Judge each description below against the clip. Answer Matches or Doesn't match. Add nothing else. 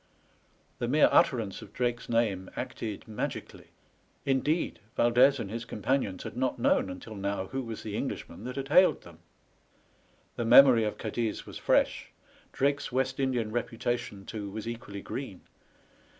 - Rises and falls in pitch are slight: Doesn't match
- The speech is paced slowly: Doesn't match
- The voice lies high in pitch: Doesn't match